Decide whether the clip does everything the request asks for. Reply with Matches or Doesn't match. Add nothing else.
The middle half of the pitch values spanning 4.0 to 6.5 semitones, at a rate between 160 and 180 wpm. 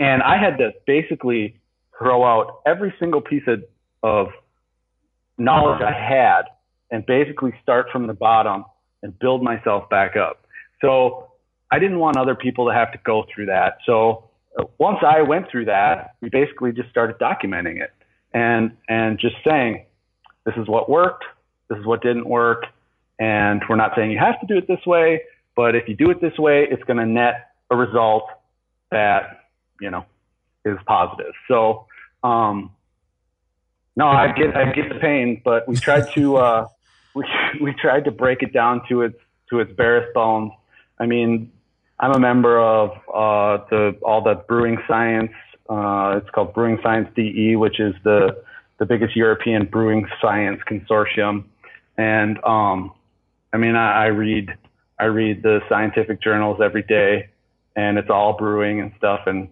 Doesn't match